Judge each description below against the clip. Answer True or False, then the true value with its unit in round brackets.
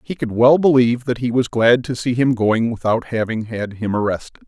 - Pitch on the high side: False (120 Hz)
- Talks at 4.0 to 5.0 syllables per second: False (5.4 syllables/s)